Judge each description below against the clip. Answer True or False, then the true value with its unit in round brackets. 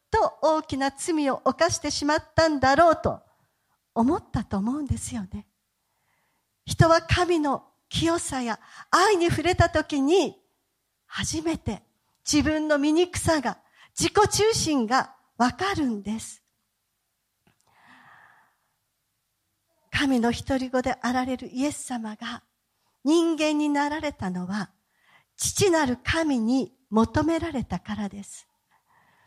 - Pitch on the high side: True (290 Hz)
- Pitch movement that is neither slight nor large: True (4.8 semitones)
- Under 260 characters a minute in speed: True (225 characters per minute)